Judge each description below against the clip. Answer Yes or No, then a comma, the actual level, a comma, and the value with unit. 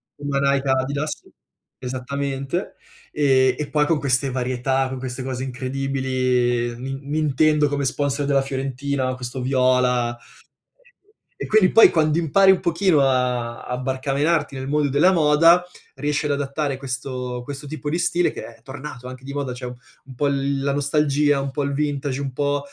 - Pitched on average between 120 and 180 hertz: Yes, medium, 140 Hz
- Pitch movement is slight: Yes, narrow, 2.3 semitones